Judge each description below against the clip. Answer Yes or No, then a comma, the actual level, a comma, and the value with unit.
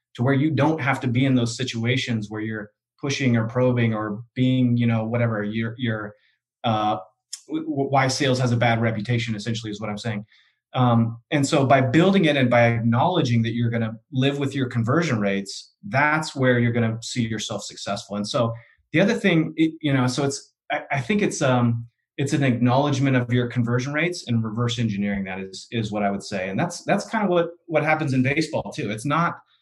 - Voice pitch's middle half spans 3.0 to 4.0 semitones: Yes, average, 3.7 semitones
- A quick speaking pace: Yes, fast, 215 wpm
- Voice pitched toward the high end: No, low, 125 Hz